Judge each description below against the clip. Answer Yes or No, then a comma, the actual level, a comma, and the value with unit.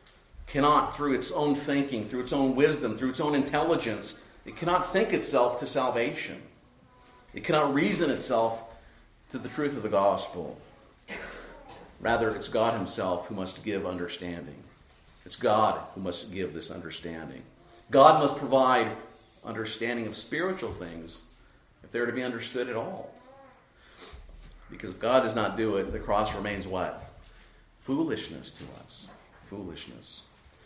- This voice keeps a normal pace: Yes, average, 145 wpm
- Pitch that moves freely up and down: Yes, wide, 5.7 semitones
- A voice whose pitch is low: Yes, low, 115 Hz